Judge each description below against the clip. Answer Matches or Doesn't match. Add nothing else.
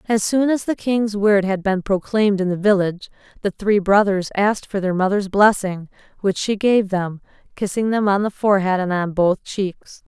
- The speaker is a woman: Matches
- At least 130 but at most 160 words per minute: Doesn't match